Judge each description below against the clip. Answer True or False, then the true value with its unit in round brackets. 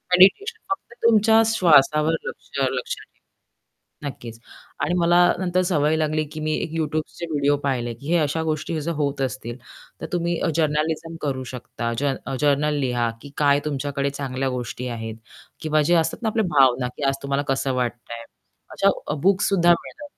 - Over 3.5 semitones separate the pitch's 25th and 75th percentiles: True (4.0 semitones)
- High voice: False (150 Hz)